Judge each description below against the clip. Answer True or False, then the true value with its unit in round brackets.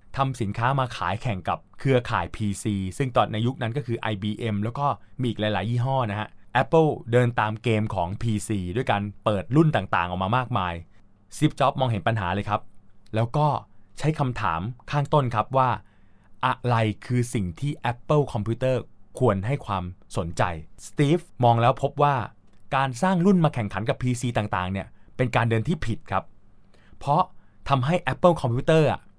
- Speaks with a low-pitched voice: True (115 Hz)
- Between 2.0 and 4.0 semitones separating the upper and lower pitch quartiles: False (4.7 semitones)